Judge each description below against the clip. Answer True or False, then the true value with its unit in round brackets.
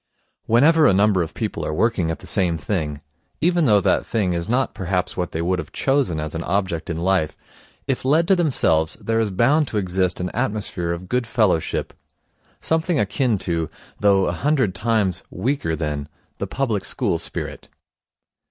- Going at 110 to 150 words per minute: False (180 wpm)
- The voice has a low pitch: True (100 Hz)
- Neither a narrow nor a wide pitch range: False (6.2 semitones)